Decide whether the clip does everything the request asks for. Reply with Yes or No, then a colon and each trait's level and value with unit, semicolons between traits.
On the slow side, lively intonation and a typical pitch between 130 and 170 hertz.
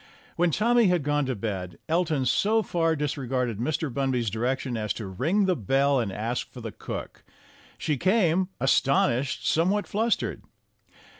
No: average, 155 wpm; wide, 6.4 semitones; medium, 140 Hz